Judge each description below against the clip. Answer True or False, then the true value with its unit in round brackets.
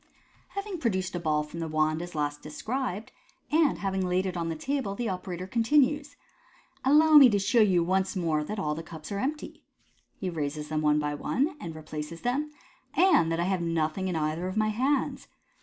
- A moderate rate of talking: False (215 wpm)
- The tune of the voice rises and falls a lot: True (7.8 semitones)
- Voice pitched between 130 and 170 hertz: False (185 Hz)